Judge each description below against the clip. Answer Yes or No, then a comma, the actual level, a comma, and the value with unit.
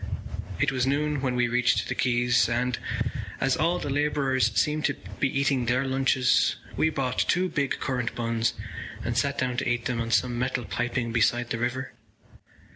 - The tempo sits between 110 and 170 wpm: No, average, 180 wpm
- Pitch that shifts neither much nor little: No, narrow, 2.2 semitones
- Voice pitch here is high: No, low, 125 Hz